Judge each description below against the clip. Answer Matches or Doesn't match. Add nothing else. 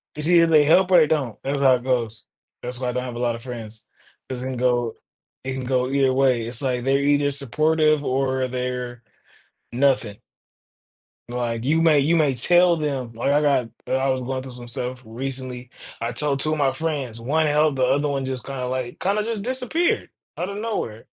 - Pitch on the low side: Matches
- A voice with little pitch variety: Doesn't match